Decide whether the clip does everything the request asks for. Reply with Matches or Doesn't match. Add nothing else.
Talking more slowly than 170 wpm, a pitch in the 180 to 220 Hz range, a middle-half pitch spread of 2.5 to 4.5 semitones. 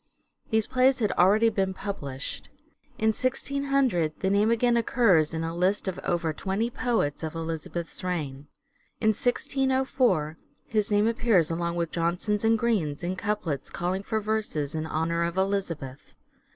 Doesn't match